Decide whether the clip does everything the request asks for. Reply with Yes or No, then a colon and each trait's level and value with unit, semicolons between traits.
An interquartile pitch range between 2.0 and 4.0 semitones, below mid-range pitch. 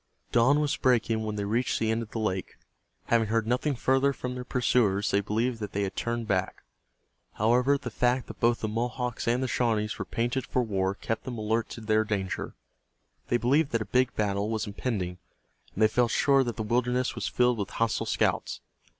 Yes: narrow, 2.6 semitones; low, 115 Hz